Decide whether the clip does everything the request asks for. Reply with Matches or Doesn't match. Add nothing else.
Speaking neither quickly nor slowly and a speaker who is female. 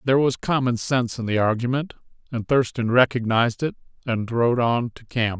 Doesn't match